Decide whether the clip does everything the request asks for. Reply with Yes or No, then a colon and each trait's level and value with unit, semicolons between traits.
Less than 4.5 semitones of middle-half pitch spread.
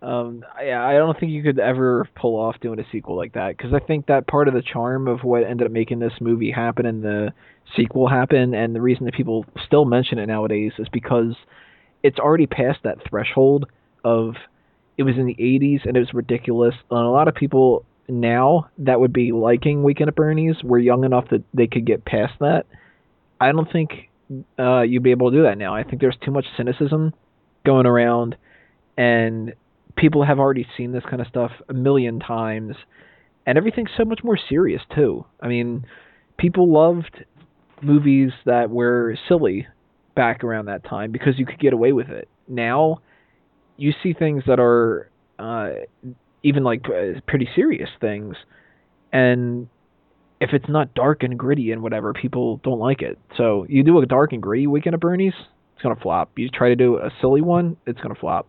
Yes: average, 3.2 semitones